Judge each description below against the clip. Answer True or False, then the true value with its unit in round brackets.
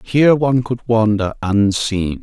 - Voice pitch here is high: False (115 Hz)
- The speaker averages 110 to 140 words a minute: True (135 wpm)